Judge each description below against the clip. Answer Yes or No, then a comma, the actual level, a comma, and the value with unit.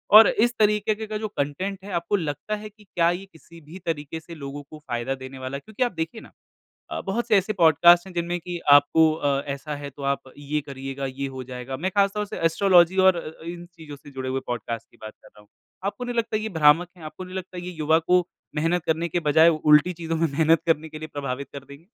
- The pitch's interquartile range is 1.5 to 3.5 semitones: No, average, 4.6 semitones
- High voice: No, medium, 160 Hz